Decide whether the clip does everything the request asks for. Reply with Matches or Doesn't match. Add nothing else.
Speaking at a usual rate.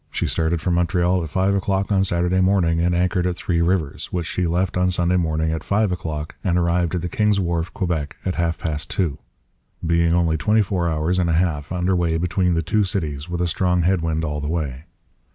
Doesn't match